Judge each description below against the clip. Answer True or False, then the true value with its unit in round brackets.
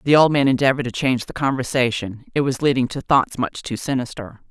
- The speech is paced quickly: True (215 wpm)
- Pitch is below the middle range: True (130 Hz)